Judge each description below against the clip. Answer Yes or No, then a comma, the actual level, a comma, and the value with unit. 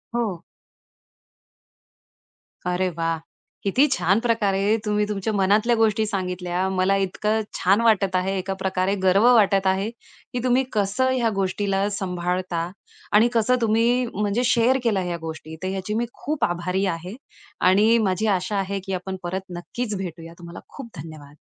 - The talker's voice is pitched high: Yes, high, 195 Hz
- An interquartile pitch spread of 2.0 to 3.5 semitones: Yes, average, 3.2 semitones